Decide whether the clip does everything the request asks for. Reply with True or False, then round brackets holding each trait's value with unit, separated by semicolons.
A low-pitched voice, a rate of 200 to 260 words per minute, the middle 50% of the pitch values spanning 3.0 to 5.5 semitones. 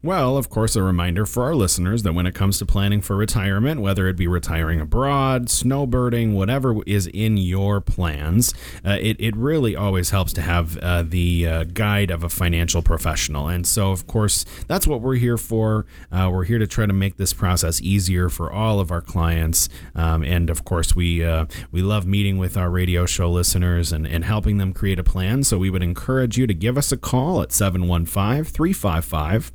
True (95 Hz; 205 wpm; 4.0 semitones)